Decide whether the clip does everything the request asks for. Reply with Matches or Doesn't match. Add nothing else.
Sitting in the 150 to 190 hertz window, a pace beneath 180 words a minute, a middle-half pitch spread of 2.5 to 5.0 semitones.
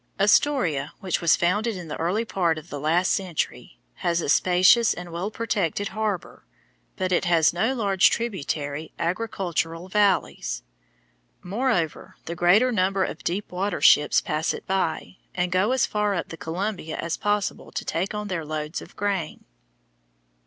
Matches